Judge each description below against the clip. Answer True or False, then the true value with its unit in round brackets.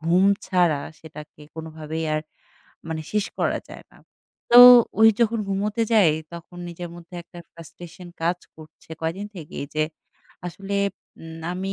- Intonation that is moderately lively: True (3.0 semitones)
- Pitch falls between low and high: True (170 Hz)